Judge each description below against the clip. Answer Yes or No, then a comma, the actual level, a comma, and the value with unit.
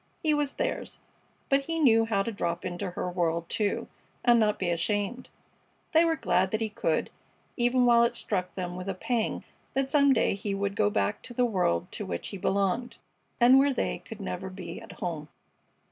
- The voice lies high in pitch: Yes, high, 210 Hz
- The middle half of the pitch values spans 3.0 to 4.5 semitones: No, average, 5.0 semitones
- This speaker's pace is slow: No, average, 200 wpm